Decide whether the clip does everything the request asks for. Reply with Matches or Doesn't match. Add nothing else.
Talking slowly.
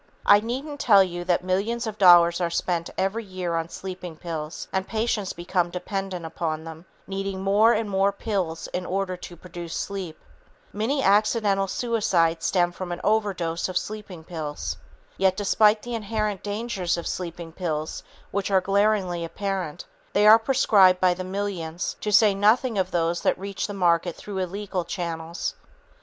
Doesn't match